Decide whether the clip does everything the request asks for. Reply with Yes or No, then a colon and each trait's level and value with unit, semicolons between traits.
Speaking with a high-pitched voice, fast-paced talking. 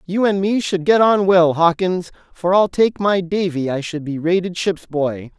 No: medium, 180 Hz; fast, 210 wpm